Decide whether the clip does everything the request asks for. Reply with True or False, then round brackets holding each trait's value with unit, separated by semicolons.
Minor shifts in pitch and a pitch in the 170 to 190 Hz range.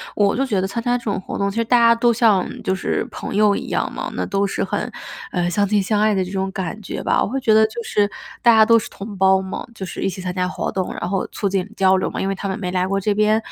False (2.3 semitones; 200 Hz)